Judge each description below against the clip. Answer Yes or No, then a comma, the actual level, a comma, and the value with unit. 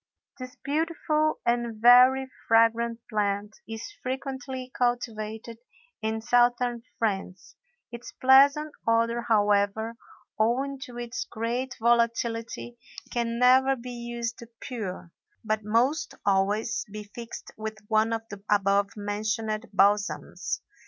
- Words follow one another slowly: Yes, slow, 110 wpm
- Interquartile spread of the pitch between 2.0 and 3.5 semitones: Yes, narrow, 2.4 semitones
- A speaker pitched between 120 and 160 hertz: No, high, 230 Hz